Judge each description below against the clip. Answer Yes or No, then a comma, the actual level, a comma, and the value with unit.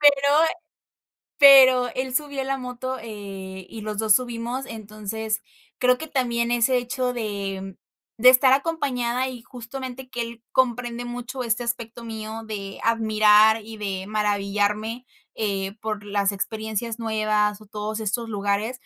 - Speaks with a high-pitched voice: Yes, high, 225 Hz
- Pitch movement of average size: Yes, average, 3.0 semitones